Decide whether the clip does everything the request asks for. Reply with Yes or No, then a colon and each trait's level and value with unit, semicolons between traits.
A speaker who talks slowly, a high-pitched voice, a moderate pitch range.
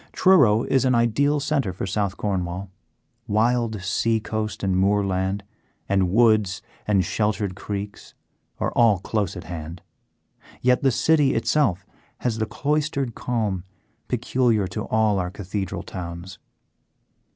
No: slow, 130 wpm; low, 105 Hz; average, 4.1 semitones